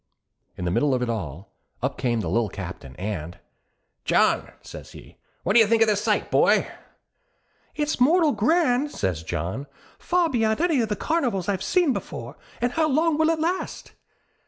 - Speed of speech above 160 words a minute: Yes, average, 180 wpm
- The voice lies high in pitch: Yes, high, 220 Hz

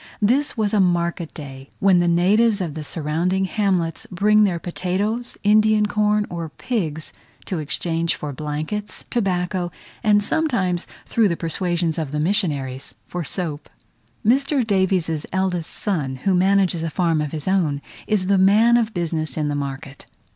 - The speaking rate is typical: Yes, average, 155 wpm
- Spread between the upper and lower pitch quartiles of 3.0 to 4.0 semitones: No, average, 4.4 semitones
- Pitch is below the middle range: No, medium, 180 Hz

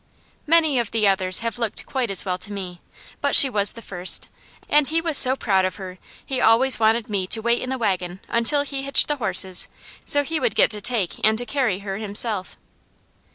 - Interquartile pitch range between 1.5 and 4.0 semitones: No, average, 5.3 semitones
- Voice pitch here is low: No, high, 225 Hz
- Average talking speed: No, fast, 215 wpm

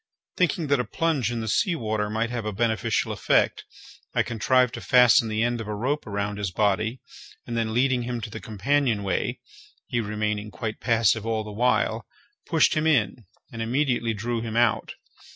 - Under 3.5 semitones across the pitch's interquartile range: Yes, narrow, 2.6 semitones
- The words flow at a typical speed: Yes, average, 190 wpm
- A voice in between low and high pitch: No, low, 115 Hz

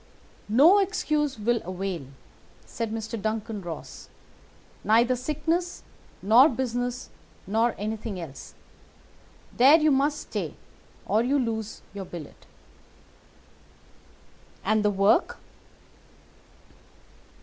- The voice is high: Yes, high, 225 Hz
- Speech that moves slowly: Yes, slow, 95 wpm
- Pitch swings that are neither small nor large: Yes, average, 4.6 semitones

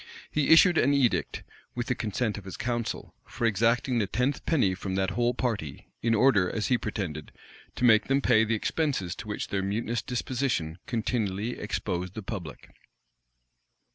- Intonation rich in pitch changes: No, average, 4.2 semitones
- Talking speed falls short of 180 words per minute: Yes, average, 170 wpm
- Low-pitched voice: Yes, low, 115 Hz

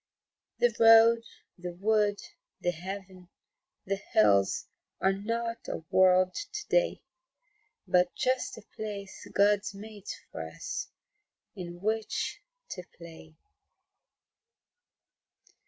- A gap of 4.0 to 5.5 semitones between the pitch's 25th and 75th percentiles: No, average, 3.6 semitones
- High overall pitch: Yes, high, 200 Hz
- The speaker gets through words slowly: Yes, slow, 100 wpm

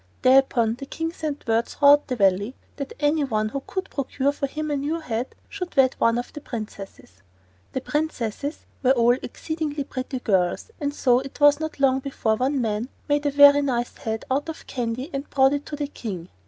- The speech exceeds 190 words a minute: Yes, average, 200 wpm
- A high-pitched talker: Yes, very high, 270 Hz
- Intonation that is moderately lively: Yes, average, 3.6 semitones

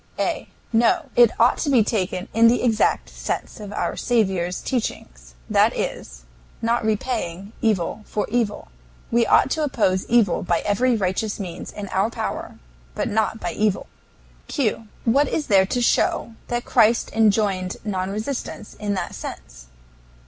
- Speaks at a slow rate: No, average, 155 wpm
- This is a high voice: Yes, high, 215 Hz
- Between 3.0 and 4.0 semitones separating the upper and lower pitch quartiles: Yes, average, 3.7 semitones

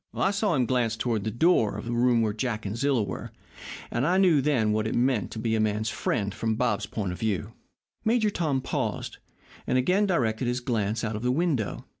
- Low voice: Yes, low, 120 Hz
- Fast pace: Yes, fast, 220 wpm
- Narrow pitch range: No, average, 4.1 semitones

